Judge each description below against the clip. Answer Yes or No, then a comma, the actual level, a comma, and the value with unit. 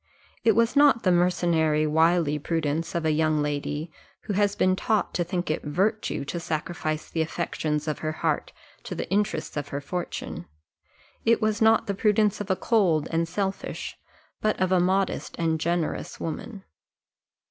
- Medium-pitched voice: Yes, medium, 175 Hz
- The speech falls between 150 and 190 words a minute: Yes, average, 170 wpm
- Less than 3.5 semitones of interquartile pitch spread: No, average, 4.5 semitones